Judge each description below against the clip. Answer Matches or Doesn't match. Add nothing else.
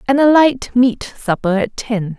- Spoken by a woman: Matches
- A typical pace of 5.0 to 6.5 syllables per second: Doesn't match